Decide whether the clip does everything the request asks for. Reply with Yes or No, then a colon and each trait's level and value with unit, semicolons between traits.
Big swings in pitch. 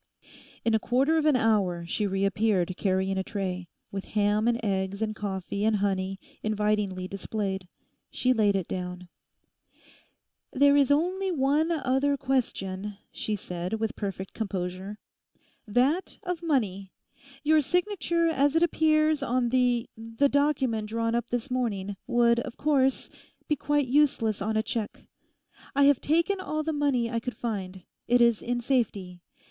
Yes: wide, 6.1 semitones